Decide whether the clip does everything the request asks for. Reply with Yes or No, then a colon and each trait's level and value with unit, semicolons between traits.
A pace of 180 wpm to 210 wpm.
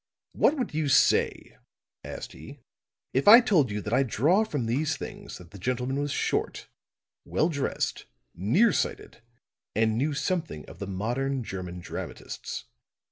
No: average, 150 wpm